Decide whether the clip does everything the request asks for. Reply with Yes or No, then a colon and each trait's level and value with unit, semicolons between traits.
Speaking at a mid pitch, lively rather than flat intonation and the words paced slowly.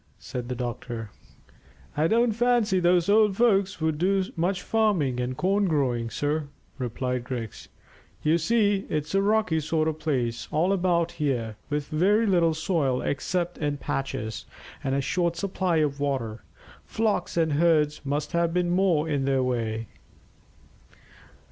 No: medium, 160 Hz; wide, 5.7 semitones; average, 150 wpm